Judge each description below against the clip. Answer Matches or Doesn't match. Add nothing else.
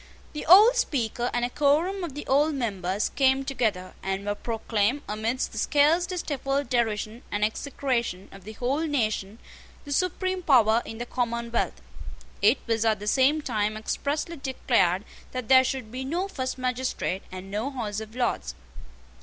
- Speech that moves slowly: Doesn't match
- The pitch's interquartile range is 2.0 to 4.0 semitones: Doesn't match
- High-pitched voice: Matches